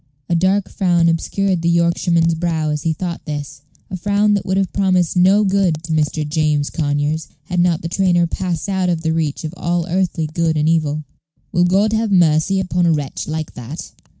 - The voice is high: No, medium, 170 Hz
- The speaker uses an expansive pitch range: No, average, 2.9 semitones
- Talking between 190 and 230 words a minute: Yes, average, 200 wpm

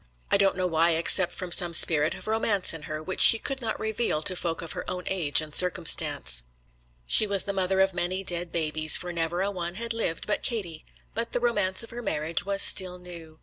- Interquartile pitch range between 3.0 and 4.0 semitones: Yes, average, 3.3 semitones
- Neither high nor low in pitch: Yes, medium, 180 Hz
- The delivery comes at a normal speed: No, fast, 225 wpm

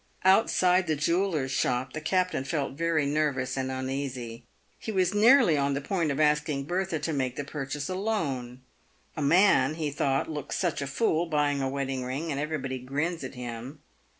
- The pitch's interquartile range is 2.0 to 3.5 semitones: No, average, 3.9 semitones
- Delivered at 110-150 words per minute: No, average, 185 wpm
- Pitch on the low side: No, medium, 145 Hz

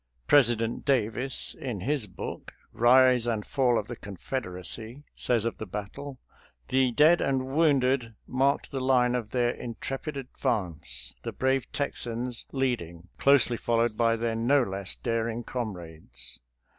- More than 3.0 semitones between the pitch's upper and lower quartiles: Yes, average, 3.4 semitones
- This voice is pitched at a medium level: No, low, 120 Hz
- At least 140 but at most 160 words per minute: Yes, average, 145 wpm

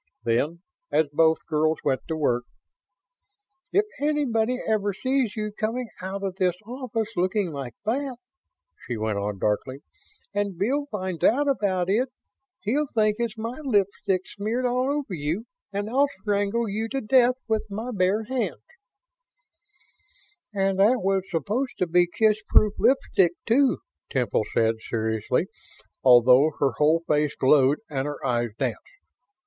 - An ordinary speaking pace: Yes, average, 145 wpm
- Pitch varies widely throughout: Yes, wide, 7.2 semitones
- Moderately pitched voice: No, high, 200 Hz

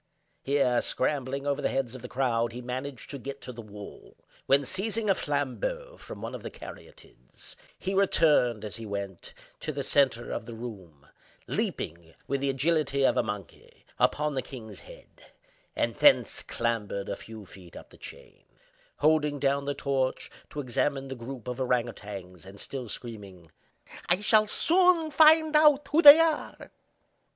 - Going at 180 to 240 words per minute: No, average, 165 wpm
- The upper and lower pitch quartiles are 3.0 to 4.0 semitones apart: No, average, 5.1 semitones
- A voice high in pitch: No, low, 135 Hz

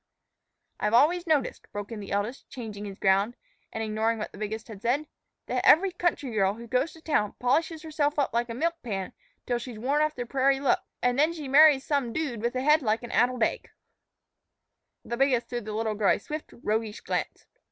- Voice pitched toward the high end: Yes, high, 245 Hz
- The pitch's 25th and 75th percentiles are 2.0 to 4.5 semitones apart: No, average, 5.1 semitones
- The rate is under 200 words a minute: No, fast, 205 wpm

